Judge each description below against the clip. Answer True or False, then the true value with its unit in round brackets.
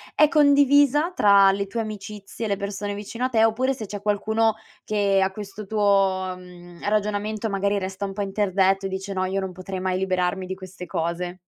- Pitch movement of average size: False (2.1 semitones)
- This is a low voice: False (200 Hz)